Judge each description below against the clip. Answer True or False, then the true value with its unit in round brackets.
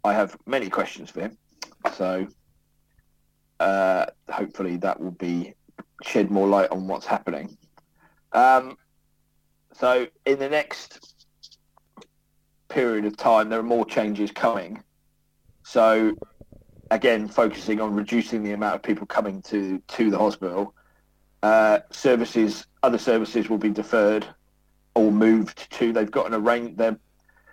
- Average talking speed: False (130 wpm)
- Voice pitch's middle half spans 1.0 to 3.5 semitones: True (2.9 semitones)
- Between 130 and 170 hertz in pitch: False (105 Hz)